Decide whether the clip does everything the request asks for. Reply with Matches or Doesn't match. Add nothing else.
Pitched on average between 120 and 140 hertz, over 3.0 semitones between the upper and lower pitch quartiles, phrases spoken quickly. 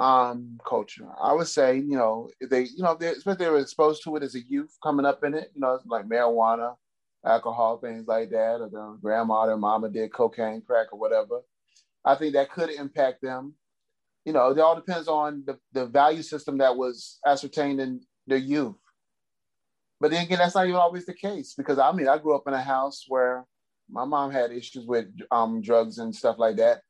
Matches